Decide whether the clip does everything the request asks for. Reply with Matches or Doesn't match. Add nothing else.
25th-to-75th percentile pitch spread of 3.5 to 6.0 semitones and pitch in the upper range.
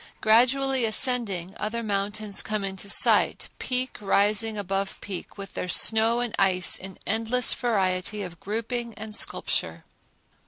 Doesn't match